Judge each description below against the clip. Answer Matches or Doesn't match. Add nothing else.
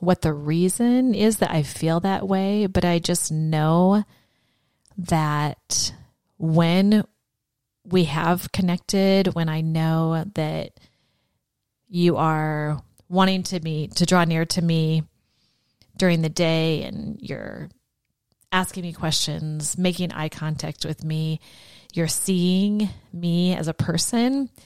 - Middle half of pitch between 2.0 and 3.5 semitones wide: Matches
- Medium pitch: Matches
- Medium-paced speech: Doesn't match